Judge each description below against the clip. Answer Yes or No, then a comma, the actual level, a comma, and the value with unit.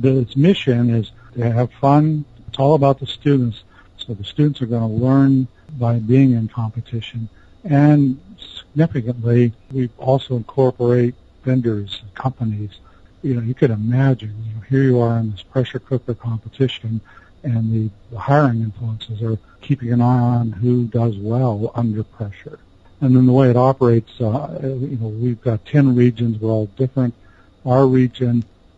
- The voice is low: Yes, low, 120 Hz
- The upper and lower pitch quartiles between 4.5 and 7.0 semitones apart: No, average, 2.8 semitones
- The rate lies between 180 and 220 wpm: No, average, 165 wpm